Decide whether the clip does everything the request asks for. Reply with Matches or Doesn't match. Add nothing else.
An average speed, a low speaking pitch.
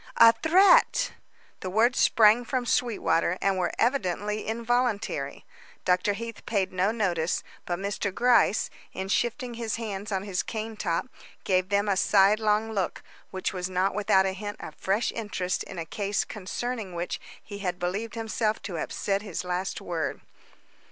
Doesn't match